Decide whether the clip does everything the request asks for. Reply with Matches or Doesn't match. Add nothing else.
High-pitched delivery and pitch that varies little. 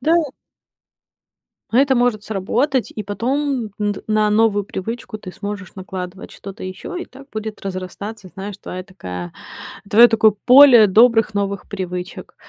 Doesn't match